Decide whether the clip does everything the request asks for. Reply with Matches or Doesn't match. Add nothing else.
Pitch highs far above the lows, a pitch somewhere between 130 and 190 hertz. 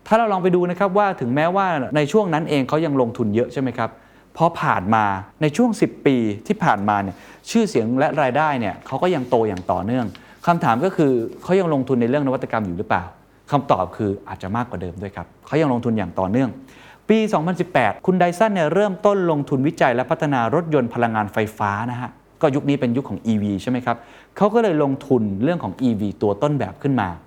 Matches